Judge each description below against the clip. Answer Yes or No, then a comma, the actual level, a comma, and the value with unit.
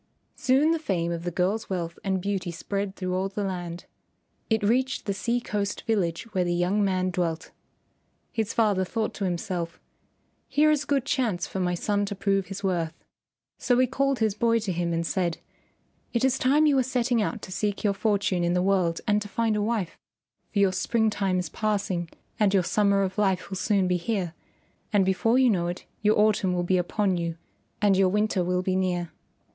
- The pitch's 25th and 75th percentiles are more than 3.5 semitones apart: No, average, 3.2 semitones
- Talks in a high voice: Yes, high, 195 Hz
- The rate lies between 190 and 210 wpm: Yes, fast, 205 wpm